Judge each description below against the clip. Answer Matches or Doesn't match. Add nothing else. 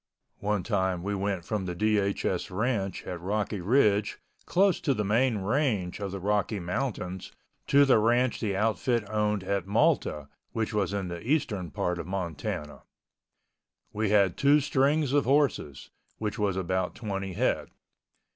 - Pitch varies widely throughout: Doesn't match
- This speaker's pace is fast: Doesn't match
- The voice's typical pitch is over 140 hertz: Doesn't match